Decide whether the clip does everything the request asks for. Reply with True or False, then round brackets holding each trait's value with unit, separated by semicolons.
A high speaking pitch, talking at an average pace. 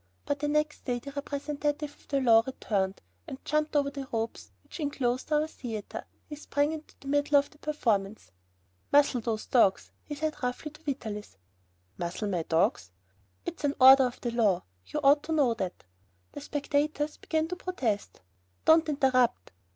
True (280 Hz; 170 wpm)